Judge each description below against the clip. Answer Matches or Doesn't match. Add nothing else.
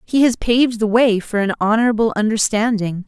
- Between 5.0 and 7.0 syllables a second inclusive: Matches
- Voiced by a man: Doesn't match